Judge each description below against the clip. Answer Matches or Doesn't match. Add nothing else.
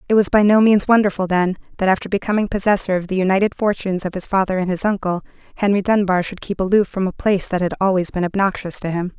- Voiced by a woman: Matches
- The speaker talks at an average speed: Doesn't match